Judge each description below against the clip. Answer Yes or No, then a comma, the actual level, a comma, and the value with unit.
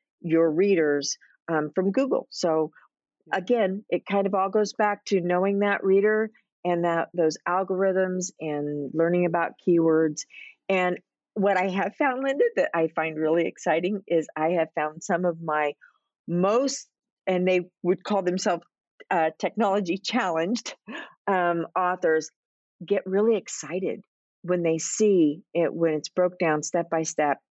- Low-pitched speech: No, medium, 180 Hz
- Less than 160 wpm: Yes, average, 150 wpm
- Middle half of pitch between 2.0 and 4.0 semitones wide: Yes, average, 3.3 semitones